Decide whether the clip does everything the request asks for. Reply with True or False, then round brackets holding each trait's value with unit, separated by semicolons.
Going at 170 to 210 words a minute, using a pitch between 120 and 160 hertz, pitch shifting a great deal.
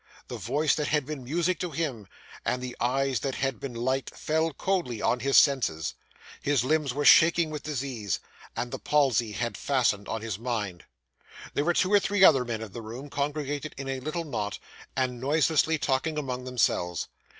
False (185 wpm; 135 Hz; 3.9 semitones)